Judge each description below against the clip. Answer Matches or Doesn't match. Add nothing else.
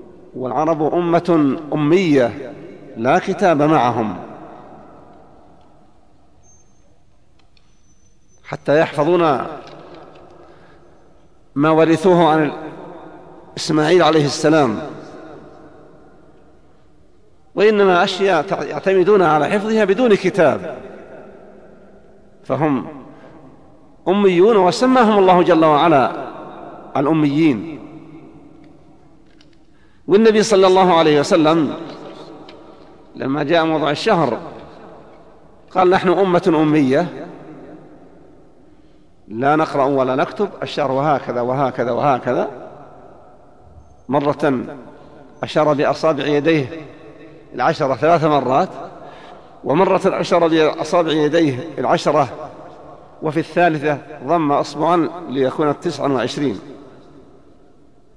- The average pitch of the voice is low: Doesn't match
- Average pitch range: Matches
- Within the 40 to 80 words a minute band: Matches